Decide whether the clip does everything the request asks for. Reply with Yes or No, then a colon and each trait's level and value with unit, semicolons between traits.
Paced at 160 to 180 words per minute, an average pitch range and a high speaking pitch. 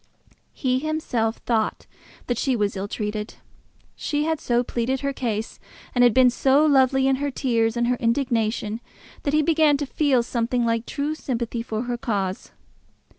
Yes: average, 170 wpm; average, 3.4 semitones; high, 245 Hz